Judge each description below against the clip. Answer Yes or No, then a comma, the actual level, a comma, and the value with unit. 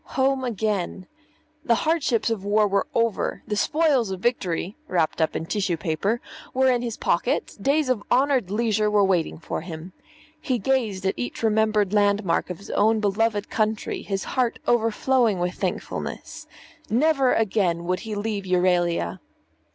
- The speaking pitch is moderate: No, high, 210 Hz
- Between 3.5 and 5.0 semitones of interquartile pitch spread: Yes, average, 4.1 semitones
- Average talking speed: Yes, average, 160 wpm